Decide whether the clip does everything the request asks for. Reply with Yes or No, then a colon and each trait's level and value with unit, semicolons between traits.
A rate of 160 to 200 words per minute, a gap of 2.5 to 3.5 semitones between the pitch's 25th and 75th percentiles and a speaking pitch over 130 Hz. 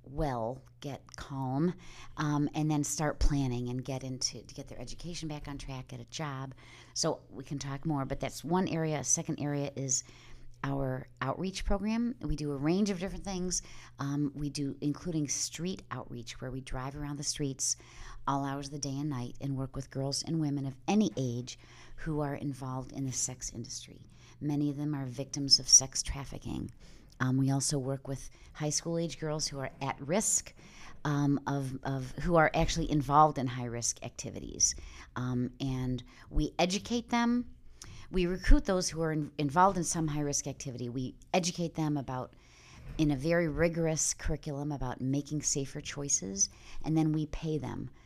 Yes: average, 180 wpm; average, 2.8 semitones; medium, 140 Hz